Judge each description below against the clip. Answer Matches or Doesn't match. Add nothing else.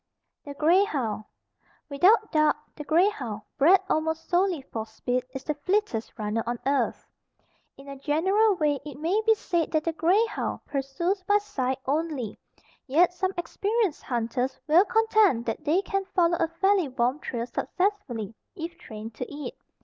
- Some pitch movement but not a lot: Doesn't match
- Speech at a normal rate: Matches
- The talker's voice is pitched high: Matches